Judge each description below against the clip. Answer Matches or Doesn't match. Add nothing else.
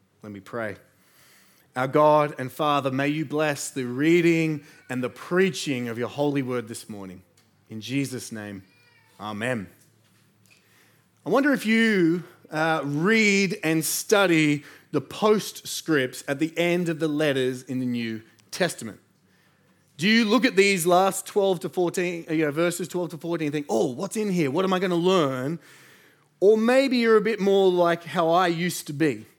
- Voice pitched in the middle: Matches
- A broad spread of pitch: Matches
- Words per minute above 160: Matches